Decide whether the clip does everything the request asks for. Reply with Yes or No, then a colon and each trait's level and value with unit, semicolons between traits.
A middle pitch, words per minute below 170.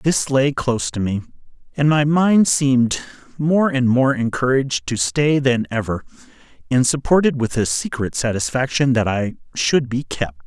No: low, 130 Hz; average, 160 wpm